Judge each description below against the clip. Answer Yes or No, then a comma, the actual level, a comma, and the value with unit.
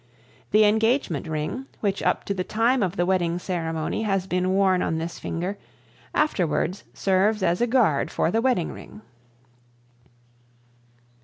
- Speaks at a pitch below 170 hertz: No, high, 190 Hz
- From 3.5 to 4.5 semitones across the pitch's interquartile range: Yes, average, 4.1 semitones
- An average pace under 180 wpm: Yes, average, 145 wpm